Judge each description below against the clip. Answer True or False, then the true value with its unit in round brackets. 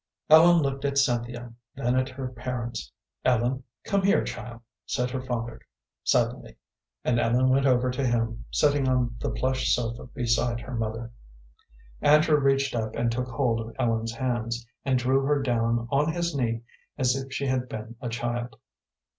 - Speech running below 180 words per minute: True (165 wpm)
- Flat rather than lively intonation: True (2.3 semitones)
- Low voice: True (125 Hz)